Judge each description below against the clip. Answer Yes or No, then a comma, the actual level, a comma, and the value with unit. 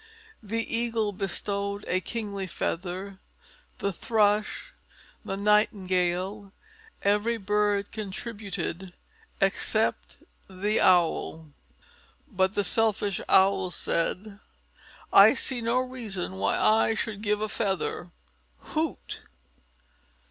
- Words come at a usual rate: No, slow, 95 wpm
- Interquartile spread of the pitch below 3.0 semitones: Yes, narrow, 2.4 semitones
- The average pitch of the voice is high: Yes, high, 200 Hz